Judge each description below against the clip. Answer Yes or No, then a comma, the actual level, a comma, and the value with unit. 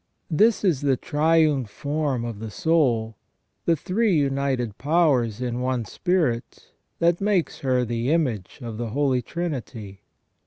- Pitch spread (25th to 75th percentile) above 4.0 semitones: Yes, wide, 5.6 semitones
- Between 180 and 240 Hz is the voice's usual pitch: No, low, 135 Hz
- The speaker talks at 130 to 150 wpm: Yes, average, 140 wpm